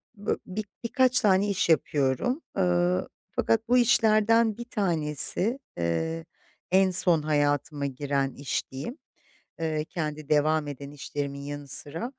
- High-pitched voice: No, medium, 160 Hz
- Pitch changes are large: Yes, wide, 6.5 semitones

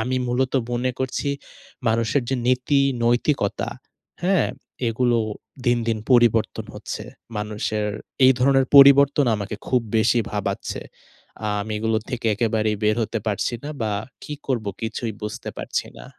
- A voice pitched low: Yes, low, 120 Hz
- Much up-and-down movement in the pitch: No, average, 3.0 semitones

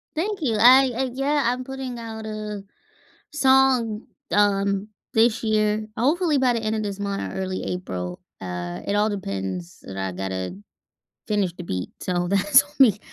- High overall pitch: Yes, high, 210 Hz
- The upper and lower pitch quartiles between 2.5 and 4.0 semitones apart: No, wide, 5.4 semitones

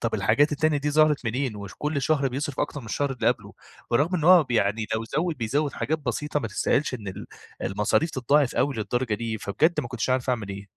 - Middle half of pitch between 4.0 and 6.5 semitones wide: Yes, average, 4.9 semitones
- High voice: No, low, 130 Hz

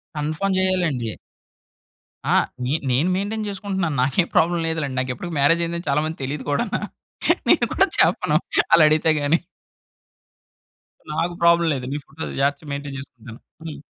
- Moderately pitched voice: Yes, medium, 155 Hz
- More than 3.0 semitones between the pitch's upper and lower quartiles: Yes, average, 3.4 semitones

